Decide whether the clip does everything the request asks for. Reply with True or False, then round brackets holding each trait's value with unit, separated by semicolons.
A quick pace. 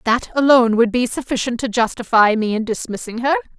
False (185 wpm)